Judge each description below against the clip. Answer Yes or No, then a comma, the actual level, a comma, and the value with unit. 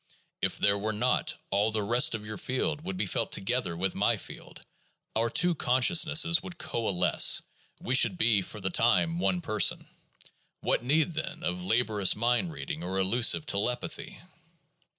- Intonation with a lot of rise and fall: Yes, wide, 7.1 semitones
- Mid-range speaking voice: No, low, 120 Hz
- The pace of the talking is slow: No, average, 165 wpm